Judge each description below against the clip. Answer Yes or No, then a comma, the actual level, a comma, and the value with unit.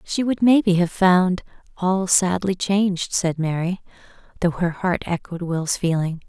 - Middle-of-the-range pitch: Yes, medium, 180 Hz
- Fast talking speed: No, average, 160 wpm